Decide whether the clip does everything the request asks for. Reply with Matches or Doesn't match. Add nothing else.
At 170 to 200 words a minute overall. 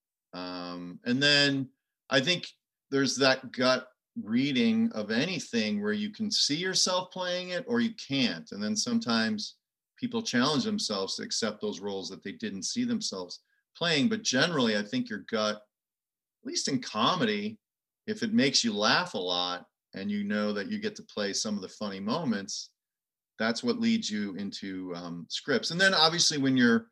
Matches